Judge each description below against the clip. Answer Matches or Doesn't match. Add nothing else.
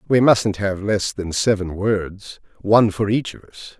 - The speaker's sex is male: Matches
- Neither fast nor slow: Matches